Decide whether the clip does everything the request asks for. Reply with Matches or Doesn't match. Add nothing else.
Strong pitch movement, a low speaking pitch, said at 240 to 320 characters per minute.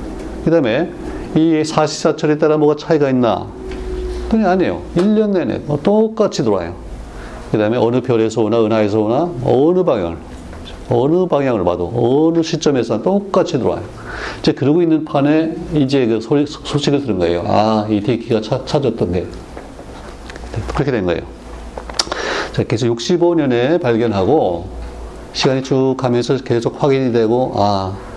Matches